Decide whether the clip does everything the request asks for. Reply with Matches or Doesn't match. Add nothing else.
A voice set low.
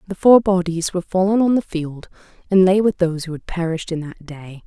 Doesn't match